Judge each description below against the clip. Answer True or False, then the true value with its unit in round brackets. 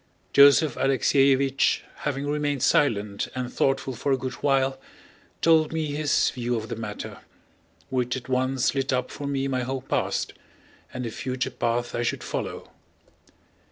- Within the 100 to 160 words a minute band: True (155 wpm)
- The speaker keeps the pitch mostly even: True (2.0 semitones)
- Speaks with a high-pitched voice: False (135 Hz)